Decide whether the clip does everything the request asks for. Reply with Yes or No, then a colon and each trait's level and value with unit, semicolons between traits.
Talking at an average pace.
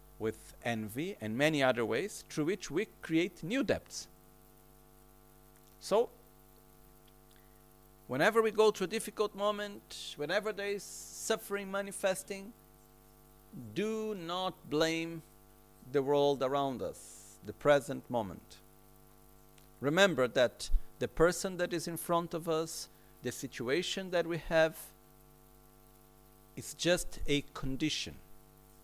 No: slow, 110 wpm